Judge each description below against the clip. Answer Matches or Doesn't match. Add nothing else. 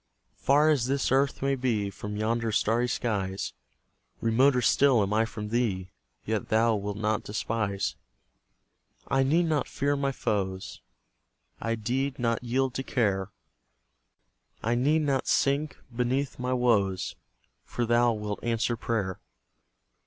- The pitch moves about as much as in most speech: Matches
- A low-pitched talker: Matches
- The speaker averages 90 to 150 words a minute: Matches